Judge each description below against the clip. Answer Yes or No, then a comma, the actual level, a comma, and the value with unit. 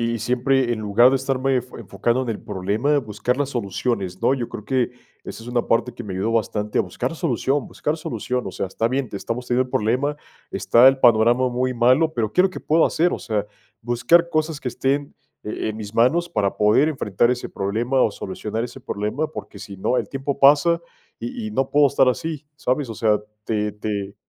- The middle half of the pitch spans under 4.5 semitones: Yes, average, 3.9 semitones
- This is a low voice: Yes, low, 120 Hz